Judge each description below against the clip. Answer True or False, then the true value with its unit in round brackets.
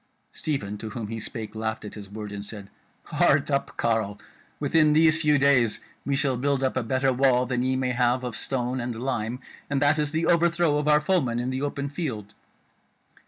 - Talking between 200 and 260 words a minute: True (205 wpm)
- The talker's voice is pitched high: False (130 Hz)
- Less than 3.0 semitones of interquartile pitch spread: False (4.3 semitones)